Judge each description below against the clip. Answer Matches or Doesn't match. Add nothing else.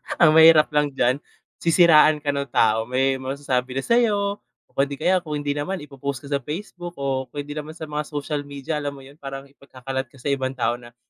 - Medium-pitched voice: Matches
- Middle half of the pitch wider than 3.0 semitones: Doesn't match